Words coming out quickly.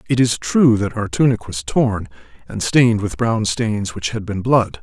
Yes: fast, 210 wpm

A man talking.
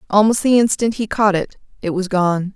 No: female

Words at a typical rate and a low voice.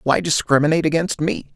No: average, 155 wpm; medium, 155 Hz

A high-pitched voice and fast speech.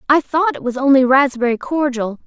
No: very high, 270 Hz; average, 185 wpm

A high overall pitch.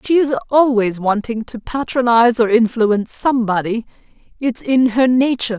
Yes: high, 235 Hz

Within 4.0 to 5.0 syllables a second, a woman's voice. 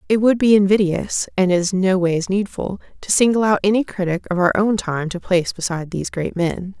No: 5.5 syllables/s; female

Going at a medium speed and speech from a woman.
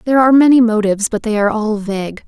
No: fast, 235 wpm; female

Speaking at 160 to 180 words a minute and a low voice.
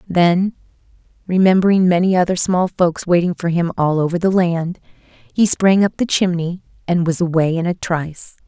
No: average, 170 wpm; medium, 175 Hz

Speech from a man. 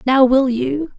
No: female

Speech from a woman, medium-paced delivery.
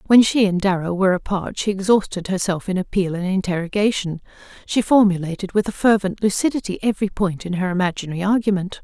Yes: female; average, 170 wpm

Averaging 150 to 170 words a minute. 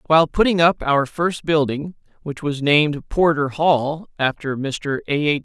Yes: average, 165 wpm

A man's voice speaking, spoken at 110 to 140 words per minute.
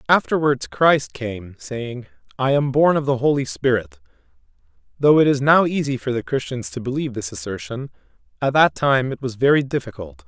No: male; average, 175 wpm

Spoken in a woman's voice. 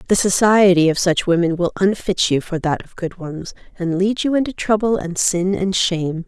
Yes: female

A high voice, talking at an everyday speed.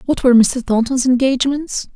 Yes: very high, 255 Hz; average, 155 wpm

